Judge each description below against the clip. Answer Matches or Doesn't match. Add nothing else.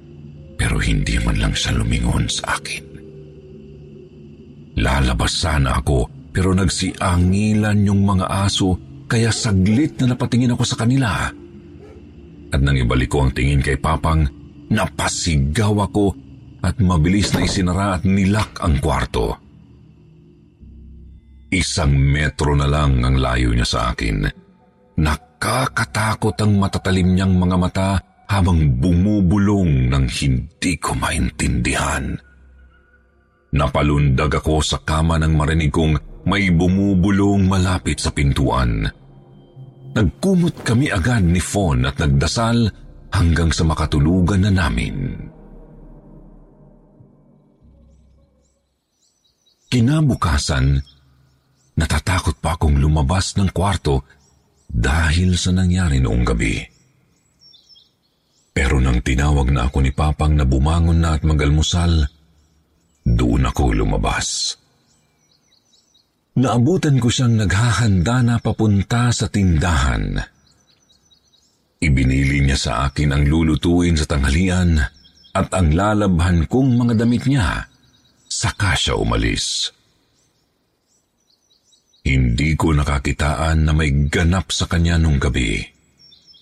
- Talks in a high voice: Doesn't match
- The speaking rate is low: Matches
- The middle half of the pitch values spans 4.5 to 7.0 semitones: Matches